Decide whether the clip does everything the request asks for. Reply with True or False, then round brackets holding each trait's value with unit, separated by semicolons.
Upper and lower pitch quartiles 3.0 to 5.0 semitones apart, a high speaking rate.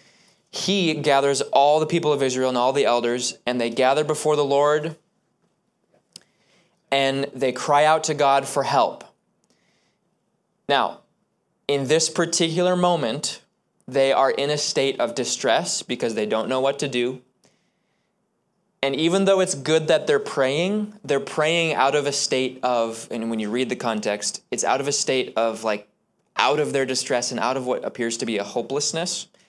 False (4.4 semitones; 175 wpm)